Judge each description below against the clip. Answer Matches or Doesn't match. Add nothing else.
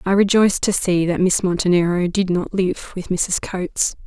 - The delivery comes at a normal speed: Matches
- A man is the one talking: Doesn't match